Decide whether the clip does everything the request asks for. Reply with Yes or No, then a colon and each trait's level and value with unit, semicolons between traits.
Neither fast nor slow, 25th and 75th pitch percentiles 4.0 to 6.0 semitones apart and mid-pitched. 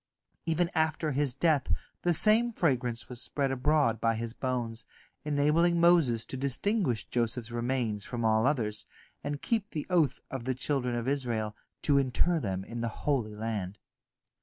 No: average, 160 wpm; average, 4.7 semitones; low, 130 Hz